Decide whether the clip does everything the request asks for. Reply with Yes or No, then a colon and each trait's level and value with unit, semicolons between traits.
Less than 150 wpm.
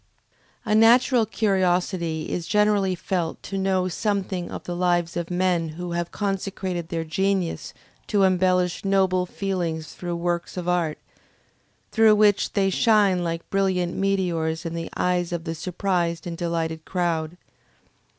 Yes: average, 140 wpm